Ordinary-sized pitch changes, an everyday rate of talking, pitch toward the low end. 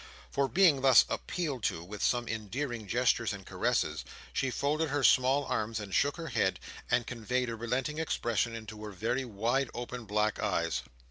Yes: average, 3.9 semitones; average, 175 wpm; low, 120 Hz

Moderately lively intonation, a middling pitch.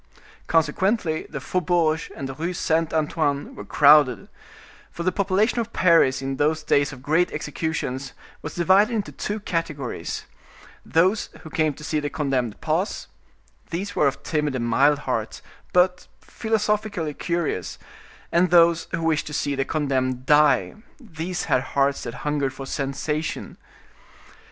Yes: average, 4.0 semitones; medium, 155 Hz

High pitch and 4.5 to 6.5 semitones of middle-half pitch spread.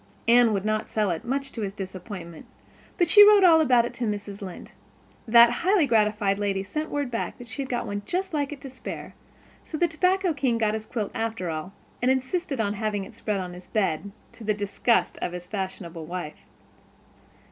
Yes: high, 220 Hz; wide, 5.6 semitones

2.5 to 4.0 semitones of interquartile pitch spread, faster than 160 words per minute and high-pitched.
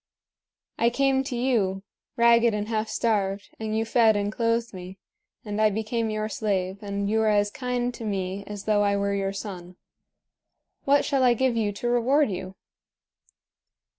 Yes: average, 2.8 semitones; average, 170 wpm; high, 215 Hz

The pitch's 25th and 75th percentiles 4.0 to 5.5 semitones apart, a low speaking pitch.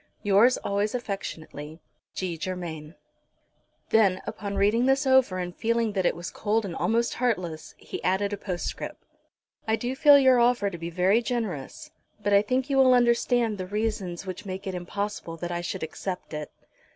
No: average, 4.6 semitones; high, 200 Hz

